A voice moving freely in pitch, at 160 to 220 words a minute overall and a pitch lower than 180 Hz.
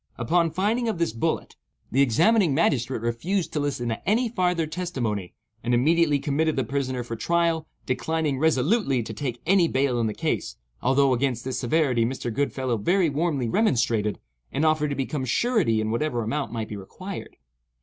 Yes: wide, 5.8 semitones; average, 170 wpm; medium, 140 Hz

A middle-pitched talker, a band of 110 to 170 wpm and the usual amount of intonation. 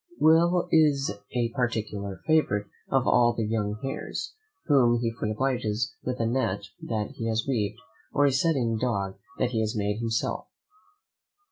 No: low, 115 Hz; average, 155 wpm; average, 3.8 semitones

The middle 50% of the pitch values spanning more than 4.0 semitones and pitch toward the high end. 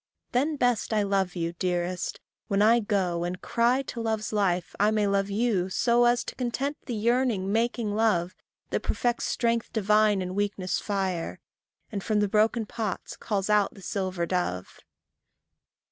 No: average, 3.7 semitones; high, 210 Hz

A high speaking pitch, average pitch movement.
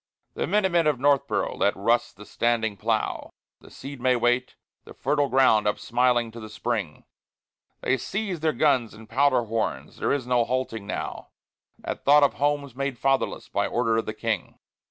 No: low, 125 Hz; average, 3.7 semitones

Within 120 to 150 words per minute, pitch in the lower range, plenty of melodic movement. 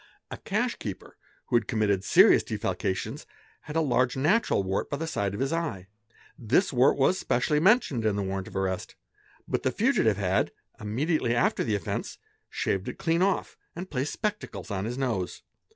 No: average, 180 wpm; low, 120 Hz; wide, 7.9 semitones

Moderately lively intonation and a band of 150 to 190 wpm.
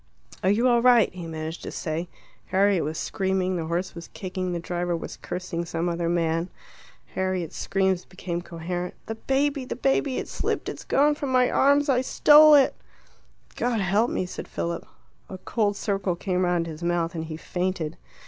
Yes: average, 4.7 semitones; average, 180 wpm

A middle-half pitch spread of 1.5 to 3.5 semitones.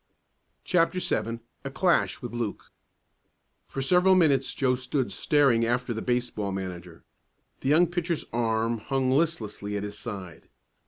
No: average, 4.9 semitones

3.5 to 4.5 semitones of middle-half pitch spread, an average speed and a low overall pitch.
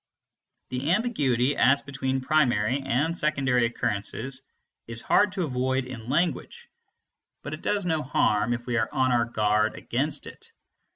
Yes: average, 4.0 semitones; average, 150 wpm; low, 130 Hz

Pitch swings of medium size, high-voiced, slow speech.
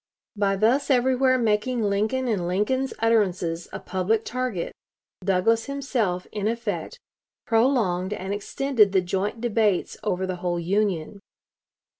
Yes: average, 4.3 semitones; high, 210 Hz; slow, 125 wpm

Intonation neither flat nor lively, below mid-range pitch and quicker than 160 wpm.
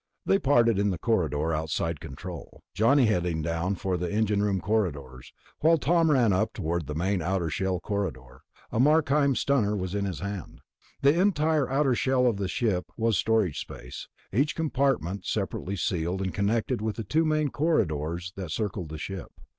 No: wide, 6.9 semitones; low, 100 Hz; average, 170 wpm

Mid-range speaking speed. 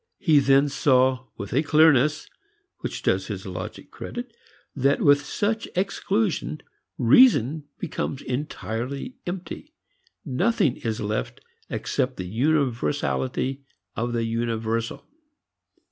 No: slow, 105 wpm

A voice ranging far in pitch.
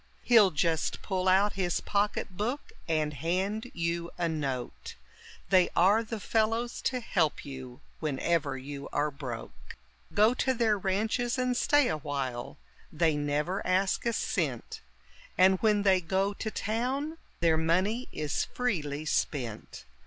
Yes: wide, 6.2 semitones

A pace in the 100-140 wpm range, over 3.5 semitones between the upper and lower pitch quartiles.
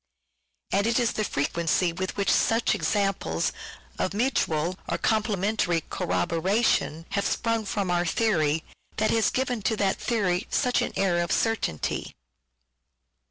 Yes: slow, 135 wpm; average, 4.3 semitones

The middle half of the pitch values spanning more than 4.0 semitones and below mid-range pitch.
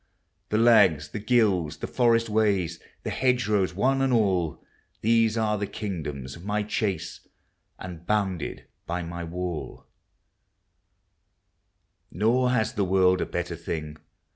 Yes: average, 4.4 semitones; low, 100 Hz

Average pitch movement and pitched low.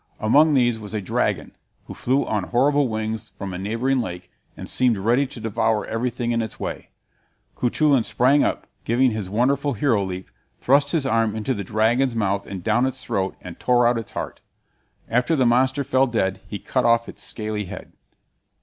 Yes: average, 3.5 semitones; low, 115 Hz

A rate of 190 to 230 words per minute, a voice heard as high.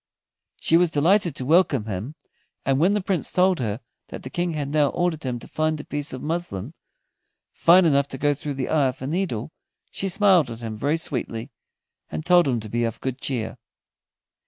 No: fast, 205 wpm; medium, 145 Hz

